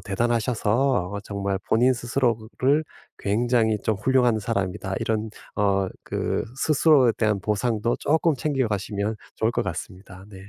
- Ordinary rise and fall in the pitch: Yes, average, 3.6 semitones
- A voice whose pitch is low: Yes, low, 110 Hz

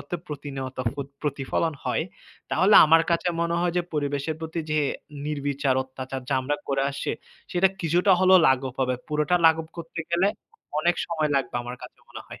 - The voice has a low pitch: No, medium, 150 Hz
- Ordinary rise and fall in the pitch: Yes, average, 3.7 semitones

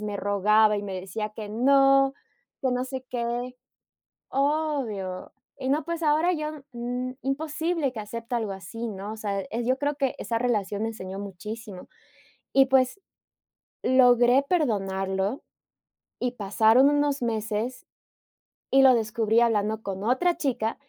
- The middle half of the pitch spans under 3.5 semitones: No, average, 4.3 semitones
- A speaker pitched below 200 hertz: No, high, 235 Hz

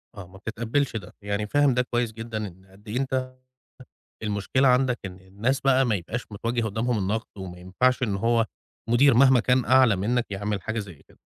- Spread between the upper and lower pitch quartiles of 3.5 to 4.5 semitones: Yes, average, 3.8 semitones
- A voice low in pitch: Yes, low, 115 Hz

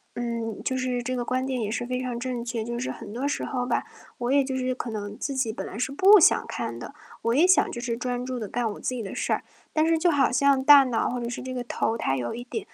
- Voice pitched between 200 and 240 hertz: No, very high, 250 Hz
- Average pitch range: No, narrow, 2.0 semitones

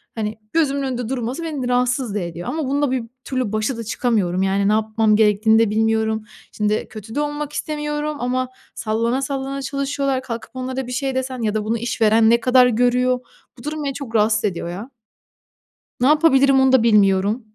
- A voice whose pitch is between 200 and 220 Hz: No, high, 245 Hz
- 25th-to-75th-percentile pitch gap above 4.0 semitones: No, average, 3.6 semitones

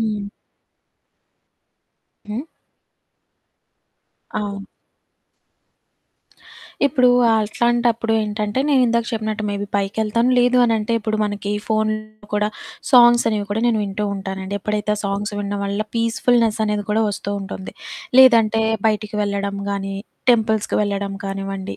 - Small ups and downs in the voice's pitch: Yes, narrow, 2.0 semitones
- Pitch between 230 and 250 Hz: No, high, 215 Hz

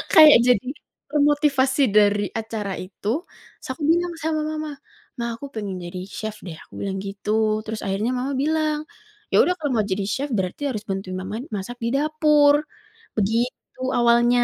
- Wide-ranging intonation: Yes, wide, 6.0 semitones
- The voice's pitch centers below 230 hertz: No, high, 235 Hz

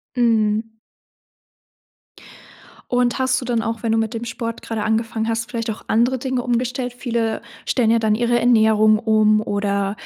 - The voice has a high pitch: Yes, high, 230 Hz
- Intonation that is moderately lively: No, narrow, 1.7 semitones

